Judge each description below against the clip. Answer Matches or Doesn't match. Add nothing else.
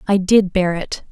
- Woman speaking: Matches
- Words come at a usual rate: Doesn't match